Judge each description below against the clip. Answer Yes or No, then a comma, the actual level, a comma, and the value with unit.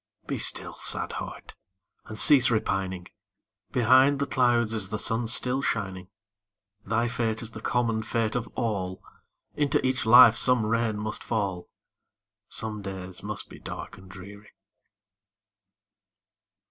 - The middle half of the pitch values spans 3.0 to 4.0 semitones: Yes, average, 3.3 semitones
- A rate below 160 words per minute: Yes, slow, 135 wpm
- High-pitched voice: No, low, 110 Hz